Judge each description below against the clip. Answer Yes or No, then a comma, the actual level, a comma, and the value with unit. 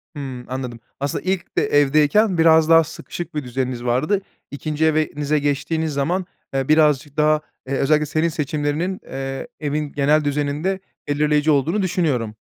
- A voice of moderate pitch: Yes, medium, 150 Hz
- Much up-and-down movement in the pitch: No, narrow, 2.4 semitones